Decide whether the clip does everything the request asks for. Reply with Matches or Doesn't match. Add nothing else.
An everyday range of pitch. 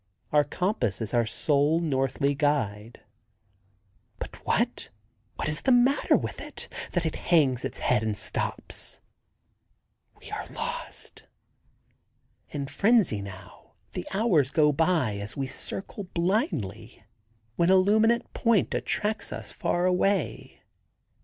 Doesn't match